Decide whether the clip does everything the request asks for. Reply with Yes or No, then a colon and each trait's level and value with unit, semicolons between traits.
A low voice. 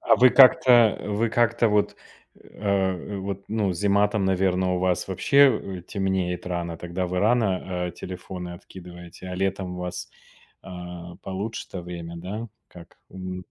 Yes: very low, 95 Hz